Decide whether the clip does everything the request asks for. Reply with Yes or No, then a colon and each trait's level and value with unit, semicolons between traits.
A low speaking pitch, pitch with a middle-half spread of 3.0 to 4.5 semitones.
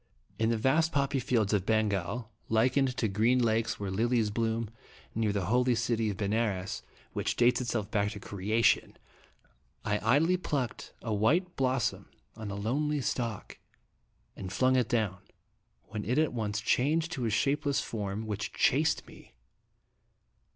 Yes: low, 115 Hz; average, 3.6 semitones